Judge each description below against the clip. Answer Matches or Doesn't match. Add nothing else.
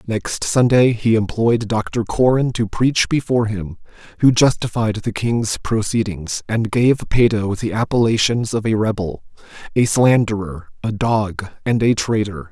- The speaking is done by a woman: Doesn't match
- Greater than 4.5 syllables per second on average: Doesn't match